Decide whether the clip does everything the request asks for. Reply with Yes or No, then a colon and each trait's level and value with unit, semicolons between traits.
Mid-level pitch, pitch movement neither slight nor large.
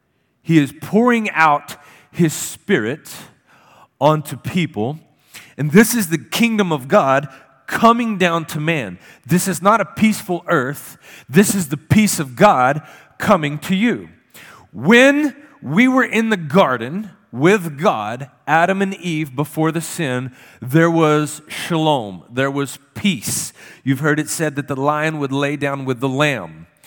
No: medium, 155 Hz; wide, 5.7 semitones